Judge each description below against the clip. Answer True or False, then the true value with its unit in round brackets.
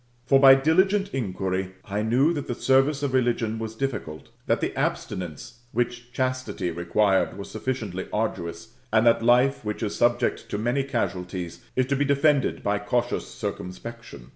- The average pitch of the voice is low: True (115 Hz)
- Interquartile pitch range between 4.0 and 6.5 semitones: True (5.1 semitones)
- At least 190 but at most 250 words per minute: False (160 wpm)